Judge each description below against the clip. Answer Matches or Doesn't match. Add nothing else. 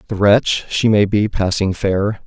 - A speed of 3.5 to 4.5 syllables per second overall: Matches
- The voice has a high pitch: Doesn't match